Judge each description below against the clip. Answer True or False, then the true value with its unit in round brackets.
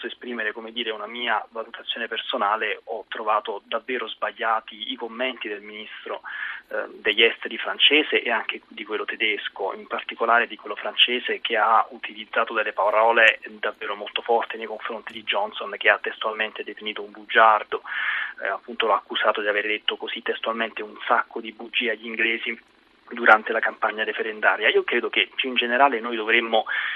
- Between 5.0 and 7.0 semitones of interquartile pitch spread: False (3.2 semitones)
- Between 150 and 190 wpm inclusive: True (160 wpm)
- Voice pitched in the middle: False (115 Hz)